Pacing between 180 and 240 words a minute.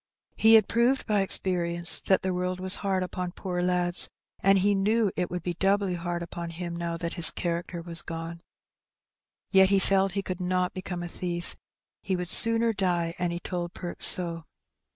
Yes: average, 190 wpm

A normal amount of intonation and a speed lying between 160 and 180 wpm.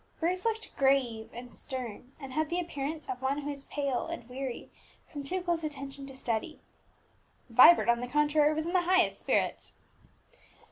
Yes: average, 3.7 semitones; average, 175 wpm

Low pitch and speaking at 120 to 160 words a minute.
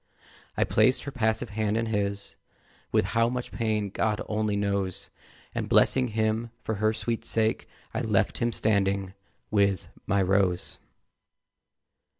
Yes: low, 110 Hz; average, 140 wpm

